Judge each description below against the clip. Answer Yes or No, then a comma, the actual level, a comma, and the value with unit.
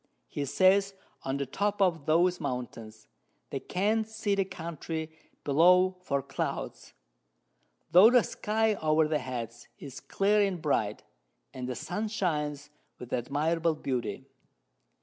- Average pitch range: No, wide, 5.9 semitones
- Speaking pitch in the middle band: Yes, medium, 160 Hz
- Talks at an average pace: No, slow, 130 wpm